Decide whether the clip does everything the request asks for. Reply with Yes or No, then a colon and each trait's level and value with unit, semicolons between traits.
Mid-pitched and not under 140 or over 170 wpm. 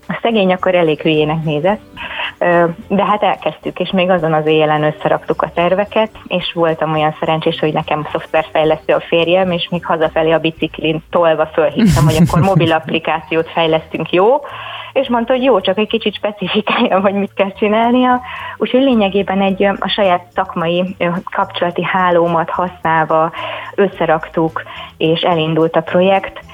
Yes: medium, 175 Hz; average, 150 wpm